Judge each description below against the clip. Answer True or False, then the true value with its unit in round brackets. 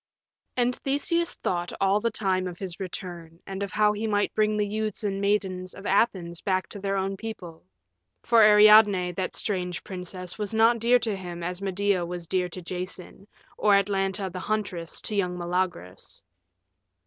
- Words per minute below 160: False (170 wpm)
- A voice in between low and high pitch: False (195 Hz)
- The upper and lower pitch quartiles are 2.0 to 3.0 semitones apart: True (2.7 semitones)